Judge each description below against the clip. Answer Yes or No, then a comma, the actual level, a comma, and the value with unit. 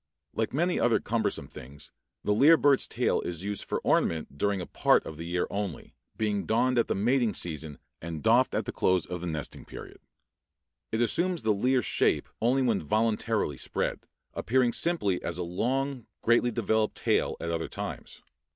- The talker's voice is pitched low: Yes, low, 110 Hz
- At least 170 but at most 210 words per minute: Yes, average, 180 wpm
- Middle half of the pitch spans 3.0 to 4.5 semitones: No, wide, 5.6 semitones